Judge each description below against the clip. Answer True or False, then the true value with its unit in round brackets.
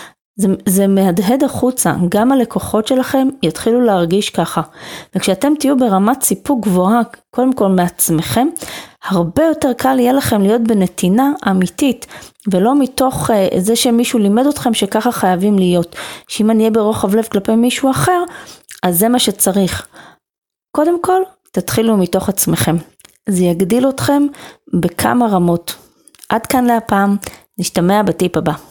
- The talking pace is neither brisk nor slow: True (135 wpm)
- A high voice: True (220 Hz)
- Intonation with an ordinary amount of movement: True (4.9 semitones)